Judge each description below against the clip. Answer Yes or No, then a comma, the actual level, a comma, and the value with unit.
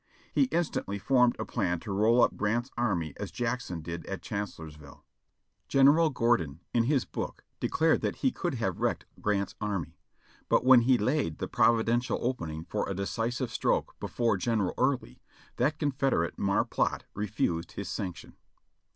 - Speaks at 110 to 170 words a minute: Yes, average, 160 wpm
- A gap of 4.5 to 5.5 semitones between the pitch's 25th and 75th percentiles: Yes, average, 5.0 semitones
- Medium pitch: No, low, 115 Hz